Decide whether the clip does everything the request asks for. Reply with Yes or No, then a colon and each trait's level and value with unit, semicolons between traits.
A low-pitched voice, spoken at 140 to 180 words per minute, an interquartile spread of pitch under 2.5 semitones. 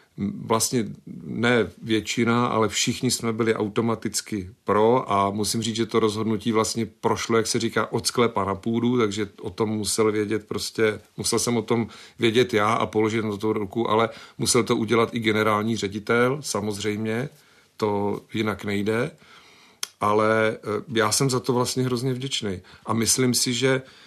Yes: low, 110 Hz; average, 160 wpm; narrow, 1.8 semitones